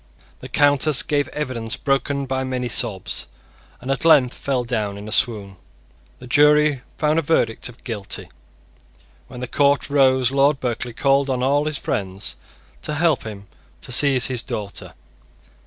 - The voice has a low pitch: Yes, low, 130 Hz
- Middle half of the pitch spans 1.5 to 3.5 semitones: Yes, average, 3.2 semitones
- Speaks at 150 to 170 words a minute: Yes, average, 155 wpm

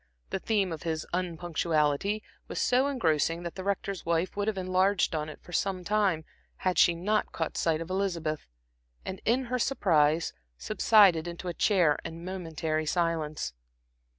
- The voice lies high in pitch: No, medium, 175 Hz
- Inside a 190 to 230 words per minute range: No, average, 160 wpm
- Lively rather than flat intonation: No, average, 3.4 semitones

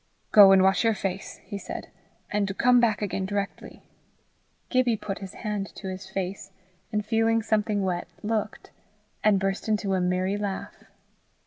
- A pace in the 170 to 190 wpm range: No, average, 155 wpm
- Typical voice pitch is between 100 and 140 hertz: No, high, 200 Hz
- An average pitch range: No, narrow, 1.9 semitones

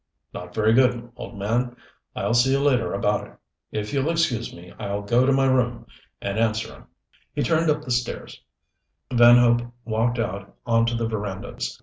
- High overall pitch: No, low, 120 Hz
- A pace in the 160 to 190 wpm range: Yes, average, 180 wpm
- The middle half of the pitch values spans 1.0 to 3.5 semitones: Yes, narrow, 2.5 semitones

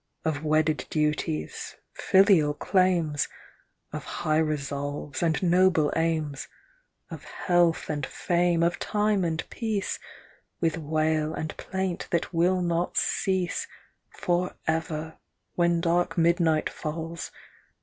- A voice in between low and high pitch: Yes, medium, 165 Hz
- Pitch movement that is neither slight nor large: No, narrow, 2.3 semitones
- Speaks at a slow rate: Yes, slow, 110 wpm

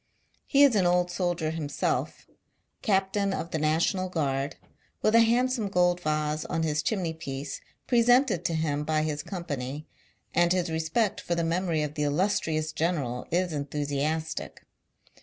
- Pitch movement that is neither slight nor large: Yes, average, 3.6 semitones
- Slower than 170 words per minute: Yes, average, 160 wpm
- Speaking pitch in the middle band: Yes, medium, 165 Hz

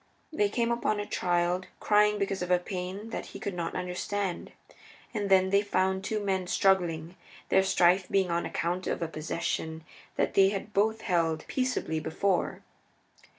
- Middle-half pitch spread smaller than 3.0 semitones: Yes, narrow, 2.5 semitones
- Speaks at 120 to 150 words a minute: No, average, 165 wpm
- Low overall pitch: No, high, 190 Hz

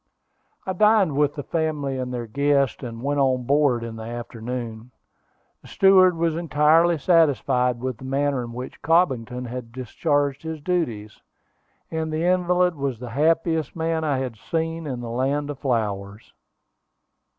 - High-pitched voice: No, medium, 140 Hz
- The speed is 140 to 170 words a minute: Yes, average, 155 wpm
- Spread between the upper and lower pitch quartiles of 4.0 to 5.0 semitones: Yes, average, 4.7 semitones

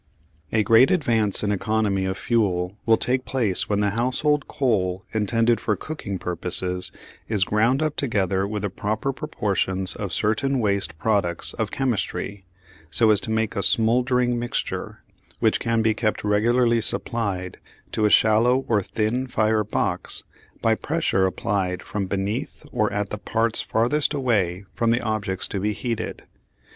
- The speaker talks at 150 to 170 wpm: Yes, average, 155 wpm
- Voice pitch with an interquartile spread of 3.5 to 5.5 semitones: No, average, 3.1 semitones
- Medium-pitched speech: No, low, 110 Hz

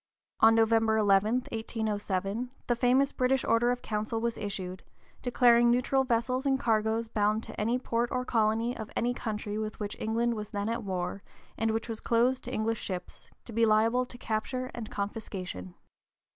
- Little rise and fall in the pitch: Yes, narrow, 2.2 semitones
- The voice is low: No, high, 225 Hz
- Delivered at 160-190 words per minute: Yes, average, 180 wpm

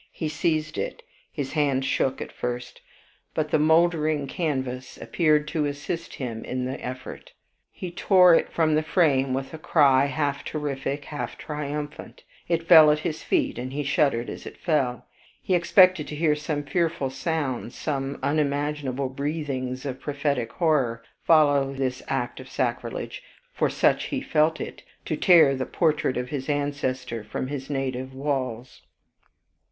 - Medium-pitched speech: Yes, medium, 145 Hz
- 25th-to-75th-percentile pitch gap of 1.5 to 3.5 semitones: Yes, average, 3.0 semitones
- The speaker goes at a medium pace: Yes, average, 155 wpm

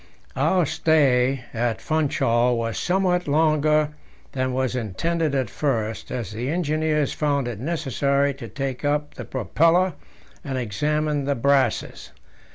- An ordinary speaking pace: No, slow, 130 wpm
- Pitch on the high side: No, medium, 140 Hz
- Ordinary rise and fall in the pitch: Yes, average, 3.5 semitones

